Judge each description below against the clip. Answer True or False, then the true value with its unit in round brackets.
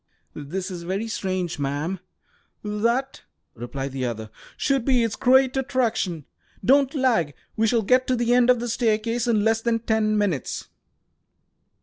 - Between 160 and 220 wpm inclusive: False (150 wpm)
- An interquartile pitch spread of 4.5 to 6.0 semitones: True (5.4 semitones)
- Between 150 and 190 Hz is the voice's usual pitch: False (220 Hz)